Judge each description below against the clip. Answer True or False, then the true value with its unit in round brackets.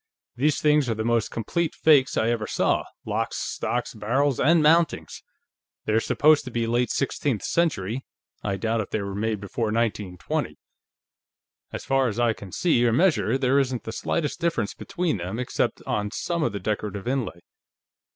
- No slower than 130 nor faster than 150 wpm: False (170 wpm)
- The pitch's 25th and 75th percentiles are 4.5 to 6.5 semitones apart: True (5.0 semitones)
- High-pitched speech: False (120 Hz)